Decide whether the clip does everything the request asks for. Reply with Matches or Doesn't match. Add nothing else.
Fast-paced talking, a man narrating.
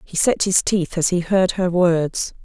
Doesn't match